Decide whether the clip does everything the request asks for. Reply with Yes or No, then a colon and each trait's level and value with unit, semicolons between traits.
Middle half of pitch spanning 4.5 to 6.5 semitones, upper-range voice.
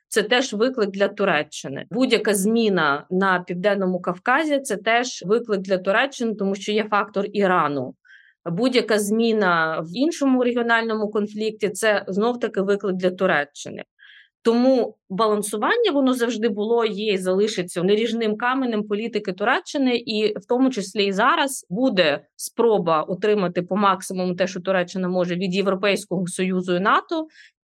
No: average, 3.6 semitones; high, 210 Hz